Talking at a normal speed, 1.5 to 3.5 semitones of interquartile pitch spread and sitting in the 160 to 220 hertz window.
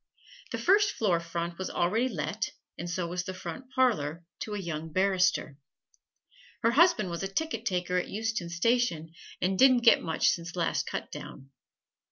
No: average, 165 wpm; average, 5.2 semitones; medium, 185 Hz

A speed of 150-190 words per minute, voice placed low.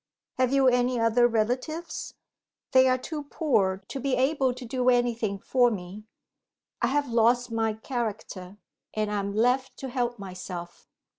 No: average, 155 wpm; high, 240 Hz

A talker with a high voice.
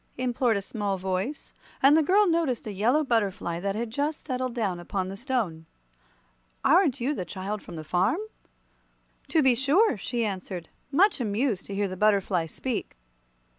Yes: high, 225 Hz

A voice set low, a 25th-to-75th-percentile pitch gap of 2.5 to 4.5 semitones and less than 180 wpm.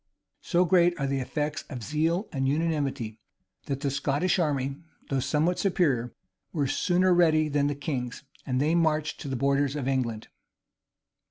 No: medium, 145 Hz; average, 3.3 semitones; average, 160 wpm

